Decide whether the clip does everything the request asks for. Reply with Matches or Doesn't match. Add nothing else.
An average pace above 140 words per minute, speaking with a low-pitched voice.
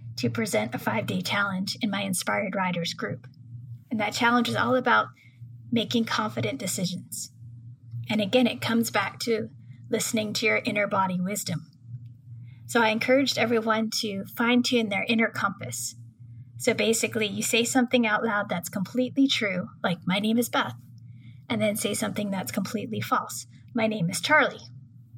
Doesn't match